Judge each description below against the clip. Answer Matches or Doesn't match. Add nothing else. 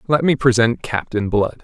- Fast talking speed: Doesn't match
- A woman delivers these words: Doesn't match